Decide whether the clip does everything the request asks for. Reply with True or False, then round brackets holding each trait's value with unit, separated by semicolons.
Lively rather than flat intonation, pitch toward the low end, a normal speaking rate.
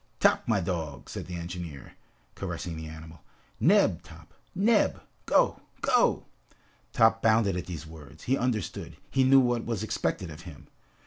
True (5.9 semitones; 90 Hz; 150 wpm)